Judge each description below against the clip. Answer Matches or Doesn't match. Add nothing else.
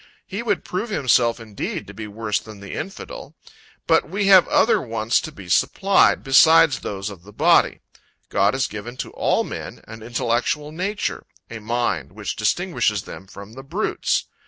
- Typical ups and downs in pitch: Doesn't match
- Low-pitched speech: Matches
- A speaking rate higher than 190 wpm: Doesn't match